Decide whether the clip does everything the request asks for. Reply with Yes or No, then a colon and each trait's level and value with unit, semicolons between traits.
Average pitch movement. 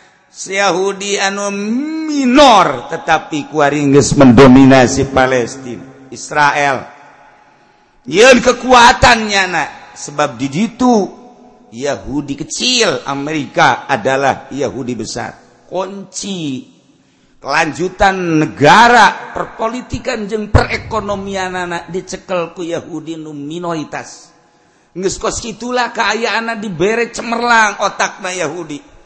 No: wide, 6.8 semitones